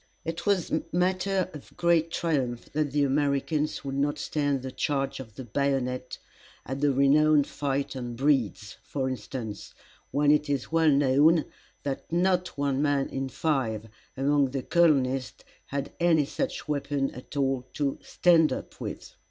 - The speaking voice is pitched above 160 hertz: No, medium, 140 Hz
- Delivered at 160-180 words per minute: No, average, 150 wpm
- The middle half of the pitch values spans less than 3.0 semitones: Yes, narrow, 2.5 semitones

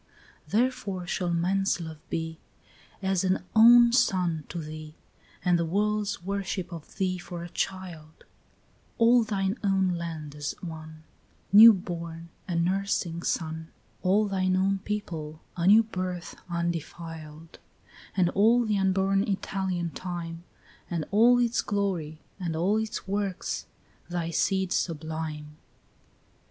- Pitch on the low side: No, medium, 180 Hz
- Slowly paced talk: Yes, slow, 130 wpm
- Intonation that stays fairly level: No, average, 3.2 semitones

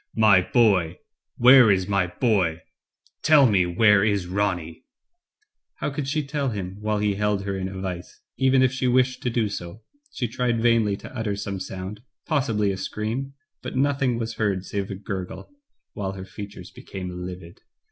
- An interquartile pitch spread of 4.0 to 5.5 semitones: Yes, average, 4.3 semitones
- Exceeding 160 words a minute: Yes, average, 180 wpm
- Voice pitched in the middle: No, low, 105 Hz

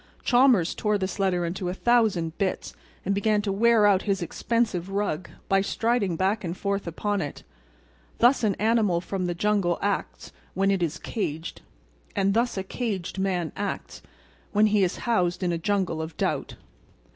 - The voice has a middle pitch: No, high, 195 Hz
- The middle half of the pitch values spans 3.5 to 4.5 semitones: No, average, 3.0 semitones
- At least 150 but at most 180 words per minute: Yes, average, 170 wpm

